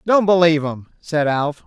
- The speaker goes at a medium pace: Yes, average, 180 wpm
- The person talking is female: No, male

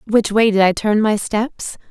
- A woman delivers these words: Yes, female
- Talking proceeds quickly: Yes, fast, 220 wpm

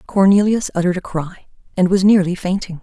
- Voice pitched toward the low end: No, medium, 185 Hz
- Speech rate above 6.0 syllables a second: No, 5.9 syllables/s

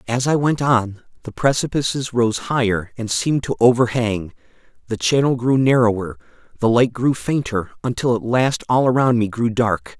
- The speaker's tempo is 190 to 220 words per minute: No, average, 170 wpm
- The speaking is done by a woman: No, male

